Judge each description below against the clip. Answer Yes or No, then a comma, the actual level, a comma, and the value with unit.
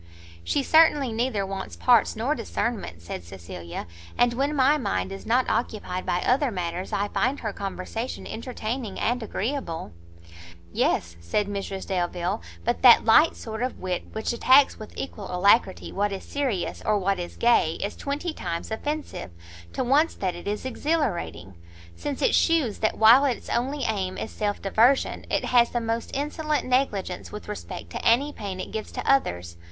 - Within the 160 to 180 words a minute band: Yes, average, 170 wpm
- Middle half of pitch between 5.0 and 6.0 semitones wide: Yes, wide, 5.5 semitones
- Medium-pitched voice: No, high, 220 Hz